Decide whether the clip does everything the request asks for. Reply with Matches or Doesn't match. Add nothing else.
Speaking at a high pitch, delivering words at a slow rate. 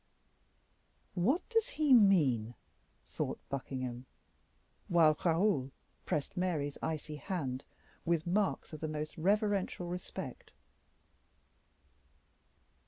Doesn't match